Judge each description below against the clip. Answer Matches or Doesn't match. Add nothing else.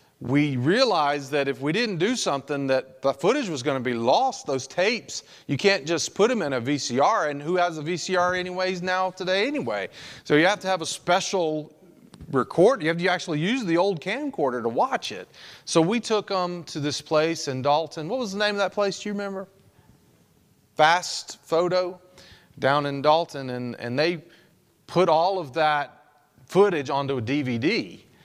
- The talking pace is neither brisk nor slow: Matches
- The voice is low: Doesn't match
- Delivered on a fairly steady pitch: Doesn't match